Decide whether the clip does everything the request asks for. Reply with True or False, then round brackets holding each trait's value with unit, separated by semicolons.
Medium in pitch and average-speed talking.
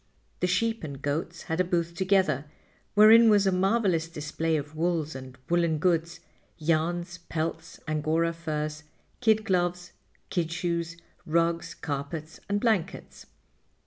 False (170 Hz; 130 wpm)